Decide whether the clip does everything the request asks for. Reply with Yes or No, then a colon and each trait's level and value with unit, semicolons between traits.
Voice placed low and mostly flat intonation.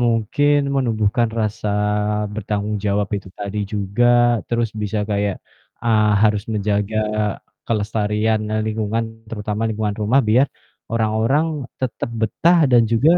Yes: low, 110 Hz; narrow, 1.8 semitones